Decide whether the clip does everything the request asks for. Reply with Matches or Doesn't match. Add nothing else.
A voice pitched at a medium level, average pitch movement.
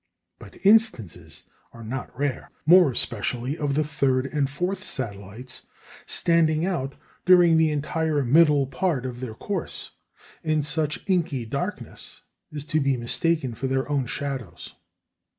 Matches